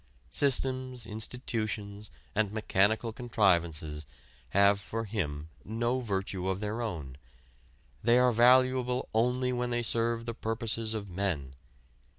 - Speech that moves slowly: Yes, slow, 120 wpm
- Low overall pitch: Yes, low, 110 Hz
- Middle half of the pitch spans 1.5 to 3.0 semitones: No, average, 3.5 semitones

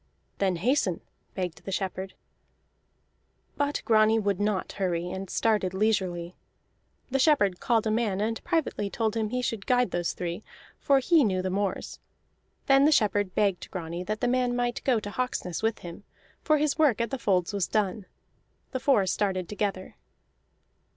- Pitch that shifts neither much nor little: Yes, average, 4.6 semitones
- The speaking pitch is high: Yes, high, 210 Hz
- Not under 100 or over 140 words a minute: No, average, 165 wpm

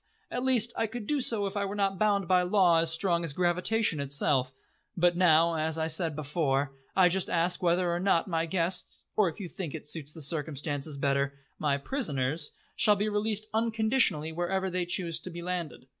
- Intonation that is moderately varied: Yes, average, 4.0 semitones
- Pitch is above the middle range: No, medium, 175 Hz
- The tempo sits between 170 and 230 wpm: Yes, average, 200 wpm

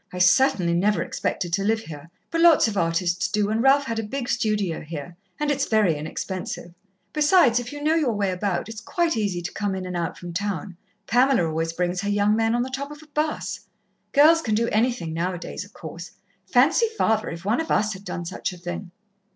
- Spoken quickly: Yes, fast, 225 wpm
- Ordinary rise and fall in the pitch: No, wide, 5.9 semitones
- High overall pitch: Yes, high, 205 Hz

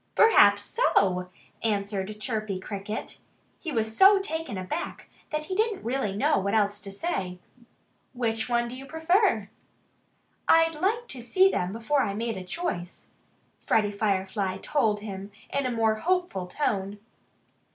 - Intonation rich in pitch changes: Yes, wide, 7.4 semitones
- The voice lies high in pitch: Yes, high, 220 Hz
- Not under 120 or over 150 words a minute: Yes, average, 145 wpm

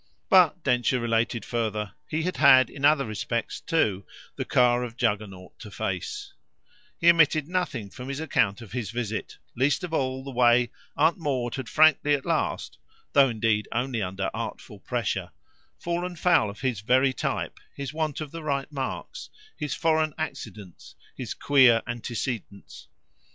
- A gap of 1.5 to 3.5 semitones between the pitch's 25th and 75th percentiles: No, average, 5.2 semitones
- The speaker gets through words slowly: No, average, 155 wpm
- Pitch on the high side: No, low, 130 Hz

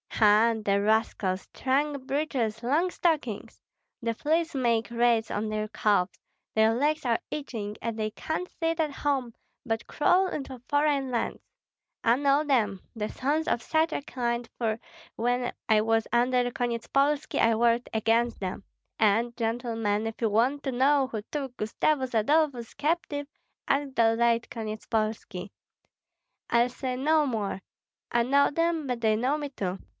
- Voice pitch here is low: No, high, 240 Hz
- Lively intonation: No, average, 4.2 semitones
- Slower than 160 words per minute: Yes, average, 150 wpm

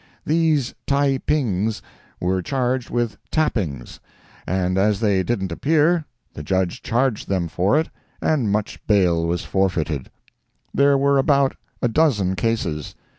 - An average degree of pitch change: No, wide, 7.0 semitones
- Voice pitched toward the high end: No, low, 110 Hz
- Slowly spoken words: Yes, slow, 125 wpm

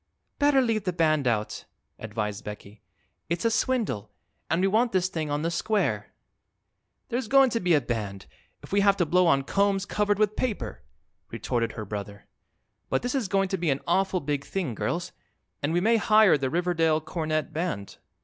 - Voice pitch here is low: No, medium, 175 Hz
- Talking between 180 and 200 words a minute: Yes, average, 185 wpm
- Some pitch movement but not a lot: No, wide, 6.8 semitones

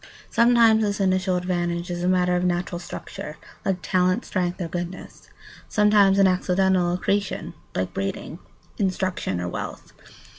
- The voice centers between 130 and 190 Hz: Yes, medium, 185 Hz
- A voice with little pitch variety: Yes, narrow, 1.8 semitones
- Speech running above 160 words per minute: No, average, 140 wpm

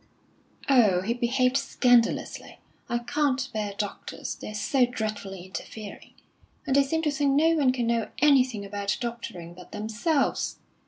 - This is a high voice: Yes, high, 240 Hz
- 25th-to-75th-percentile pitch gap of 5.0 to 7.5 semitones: No, average, 4.6 semitones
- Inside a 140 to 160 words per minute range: Yes, average, 145 wpm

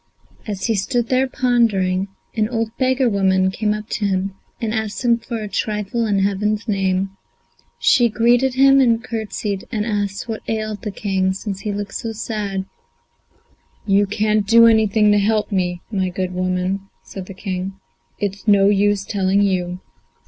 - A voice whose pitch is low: No, high, 205 Hz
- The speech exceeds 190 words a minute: No, average, 165 wpm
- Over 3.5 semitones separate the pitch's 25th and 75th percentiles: No, average, 2.7 semitones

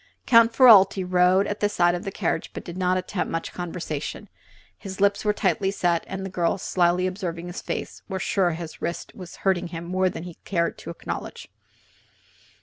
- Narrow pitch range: Yes, narrow, 1.9 semitones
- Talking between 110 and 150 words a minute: No, average, 195 wpm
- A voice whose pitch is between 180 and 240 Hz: Yes, medium, 185 Hz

